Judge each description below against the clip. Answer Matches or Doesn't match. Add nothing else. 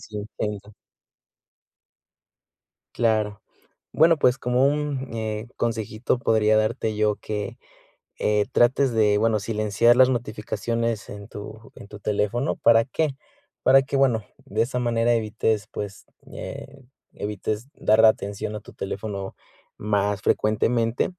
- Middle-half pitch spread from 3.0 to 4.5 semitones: Doesn't match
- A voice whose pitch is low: Matches